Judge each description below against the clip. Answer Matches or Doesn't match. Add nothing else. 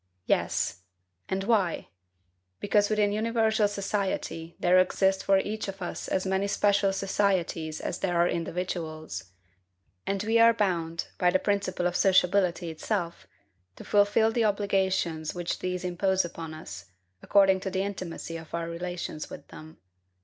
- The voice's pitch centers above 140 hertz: Matches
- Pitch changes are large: Doesn't match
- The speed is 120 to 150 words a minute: Matches